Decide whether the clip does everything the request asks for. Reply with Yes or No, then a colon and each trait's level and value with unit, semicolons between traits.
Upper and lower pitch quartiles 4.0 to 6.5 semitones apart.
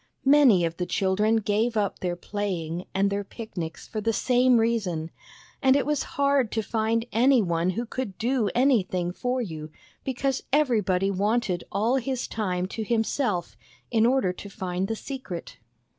Yes: average, 5.1 semitones